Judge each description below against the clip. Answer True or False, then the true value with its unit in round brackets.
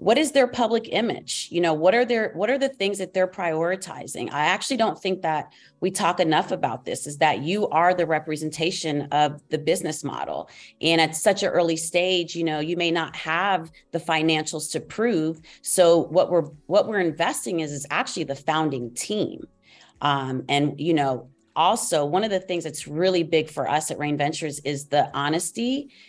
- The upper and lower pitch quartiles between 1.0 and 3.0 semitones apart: False (3.4 semitones)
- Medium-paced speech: True (195 wpm)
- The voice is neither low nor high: True (165 Hz)